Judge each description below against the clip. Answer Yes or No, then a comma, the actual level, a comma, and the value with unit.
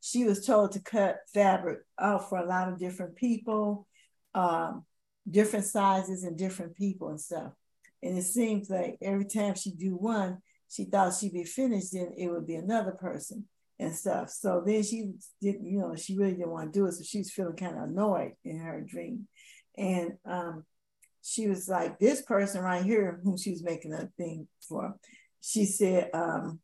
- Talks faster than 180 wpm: Yes, average, 190 wpm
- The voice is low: No, high, 195 Hz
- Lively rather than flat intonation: No, narrow, 2.5 semitones